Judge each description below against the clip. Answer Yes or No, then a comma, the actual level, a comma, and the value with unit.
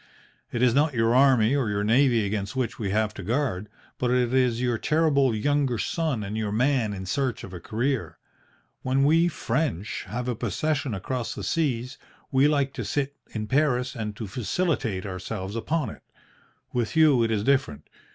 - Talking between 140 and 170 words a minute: No, average, 180 wpm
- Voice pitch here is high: No, low, 125 Hz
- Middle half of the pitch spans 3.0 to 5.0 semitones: Yes, average, 4.5 semitones